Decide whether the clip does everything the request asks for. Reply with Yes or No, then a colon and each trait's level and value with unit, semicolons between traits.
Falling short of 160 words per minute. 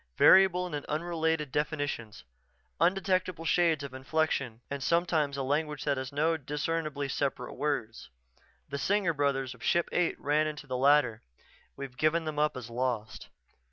Yes: average, 150 wpm